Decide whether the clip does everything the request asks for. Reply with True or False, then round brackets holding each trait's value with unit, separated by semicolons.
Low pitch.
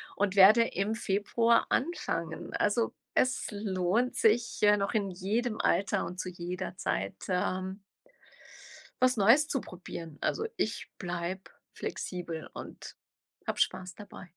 False (195 Hz)